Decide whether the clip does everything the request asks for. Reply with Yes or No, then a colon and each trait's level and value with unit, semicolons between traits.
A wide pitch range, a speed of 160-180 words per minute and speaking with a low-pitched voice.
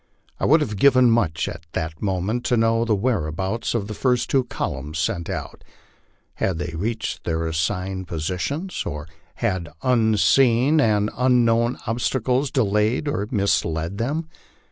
No: wide, 5.9 semitones; average, 145 wpm; low, 110 Hz